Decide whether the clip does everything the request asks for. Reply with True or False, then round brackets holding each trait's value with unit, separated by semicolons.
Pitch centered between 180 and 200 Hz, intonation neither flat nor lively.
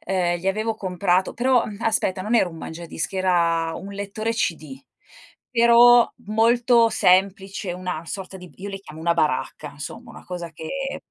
True (190 Hz; 4.6 semitones)